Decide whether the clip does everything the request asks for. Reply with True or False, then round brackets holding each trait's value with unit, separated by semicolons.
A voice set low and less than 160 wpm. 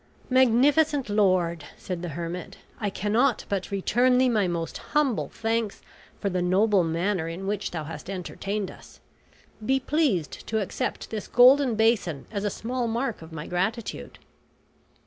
False (205 Hz; 150 wpm)